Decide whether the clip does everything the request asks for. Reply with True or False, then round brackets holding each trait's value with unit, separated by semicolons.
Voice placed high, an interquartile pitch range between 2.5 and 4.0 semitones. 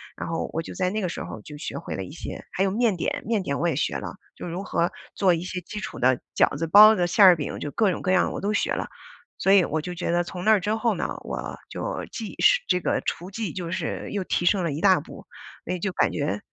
False (180 Hz; 3.5 semitones)